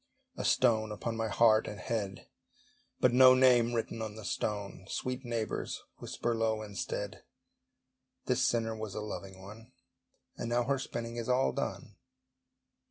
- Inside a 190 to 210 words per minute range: No, average, 150 wpm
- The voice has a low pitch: Yes, low, 115 Hz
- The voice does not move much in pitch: Yes, narrow, 2.0 semitones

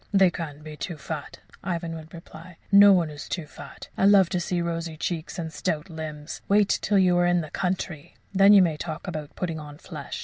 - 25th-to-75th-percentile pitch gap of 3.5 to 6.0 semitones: No, average, 2.9 semitones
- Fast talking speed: Yes, fast, 210 wpm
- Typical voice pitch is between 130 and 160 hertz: No, medium, 170 Hz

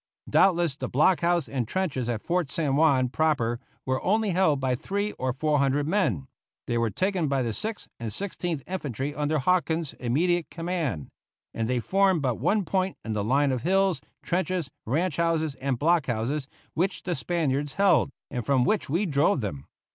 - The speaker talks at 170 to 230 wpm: Yes, average, 180 wpm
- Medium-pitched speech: Yes, medium, 150 Hz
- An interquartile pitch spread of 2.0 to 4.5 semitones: No, wide, 5.5 semitones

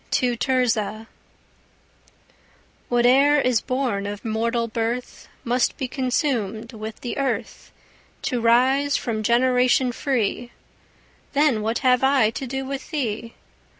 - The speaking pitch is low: No, high, 245 Hz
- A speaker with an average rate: No, slow, 115 wpm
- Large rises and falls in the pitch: No, average, 2.8 semitones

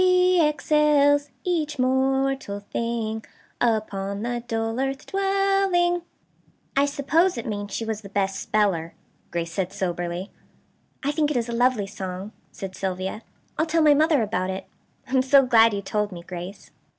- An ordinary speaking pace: Yes, average, 160 wpm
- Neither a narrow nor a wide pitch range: No, wide, 6.6 semitones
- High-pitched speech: Yes, high, 235 Hz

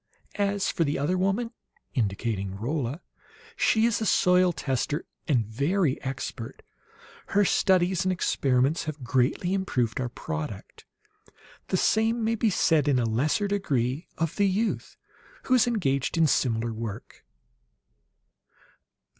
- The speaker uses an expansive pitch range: Yes, wide, 7.4 semitones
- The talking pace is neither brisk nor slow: No, slow, 130 wpm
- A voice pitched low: No, medium, 155 Hz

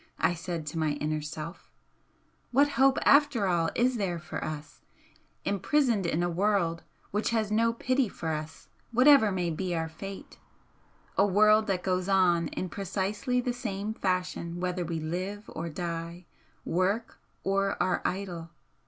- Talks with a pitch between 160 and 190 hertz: Yes, medium, 185 Hz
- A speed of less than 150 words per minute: No, average, 155 wpm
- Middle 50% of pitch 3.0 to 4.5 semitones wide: Yes, average, 4.0 semitones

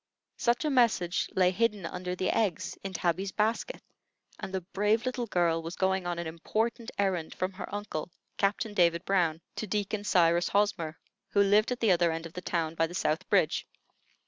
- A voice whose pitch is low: No, high, 190 Hz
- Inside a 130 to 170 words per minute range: No, average, 190 wpm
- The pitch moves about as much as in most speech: Yes, average, 3.5 semitones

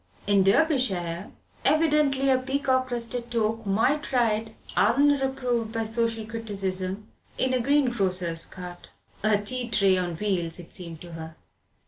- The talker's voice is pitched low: No, high, 225 Hz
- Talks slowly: Yes, slow, 130 wpm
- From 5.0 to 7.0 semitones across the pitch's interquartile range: Yes, average, 5.3 semitones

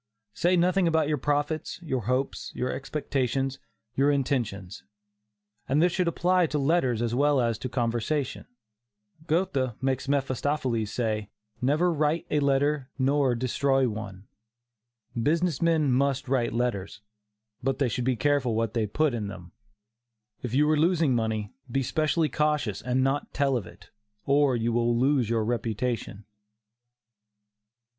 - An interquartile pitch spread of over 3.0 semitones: Yes, average, 3.9 semitones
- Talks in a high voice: No, low, 135 Hz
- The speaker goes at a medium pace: Yes, average, 145 wpm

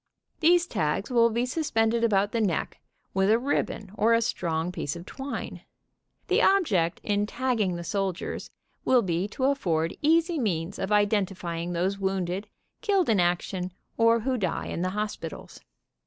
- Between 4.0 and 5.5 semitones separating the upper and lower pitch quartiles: Yes, average, 4.8 semitones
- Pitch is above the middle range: Yes, high, 205 Hz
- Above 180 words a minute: No, average, 155 wpm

